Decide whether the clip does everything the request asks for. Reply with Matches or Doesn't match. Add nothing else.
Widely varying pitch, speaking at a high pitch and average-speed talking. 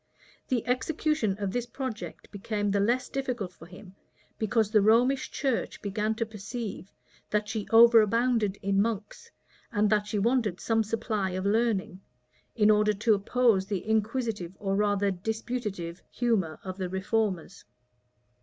Doesn't match